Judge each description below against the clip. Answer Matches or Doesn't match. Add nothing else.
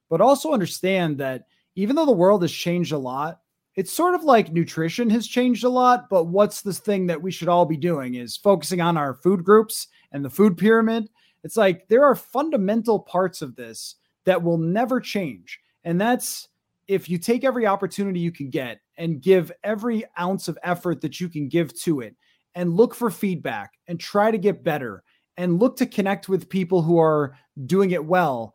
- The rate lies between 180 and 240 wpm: Matches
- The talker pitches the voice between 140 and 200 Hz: Matches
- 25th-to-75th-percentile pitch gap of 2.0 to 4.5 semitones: Matches